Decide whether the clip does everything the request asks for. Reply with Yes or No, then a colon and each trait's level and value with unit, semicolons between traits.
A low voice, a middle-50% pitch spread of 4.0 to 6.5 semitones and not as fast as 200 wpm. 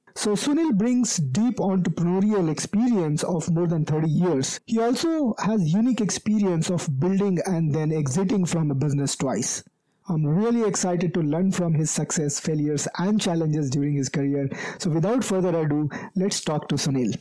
No: medium, 175 Hz; average, 4.8 semitones; average, 165 wpm